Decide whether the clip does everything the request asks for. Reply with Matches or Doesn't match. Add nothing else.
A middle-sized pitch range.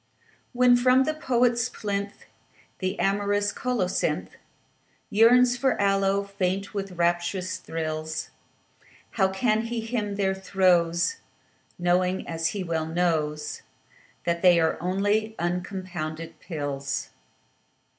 Matches